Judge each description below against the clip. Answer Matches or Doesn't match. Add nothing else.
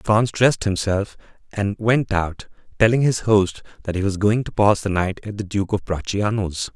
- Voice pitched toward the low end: Matches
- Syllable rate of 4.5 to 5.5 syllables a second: Matches